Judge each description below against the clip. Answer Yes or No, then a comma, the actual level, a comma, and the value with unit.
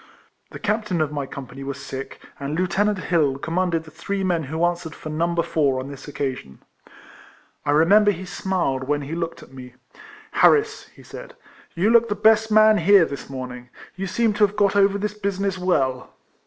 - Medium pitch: Yes, medium, 170 Hz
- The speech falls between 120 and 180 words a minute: No, average, 195 wpm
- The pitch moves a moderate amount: No, wide, 6.3 semitones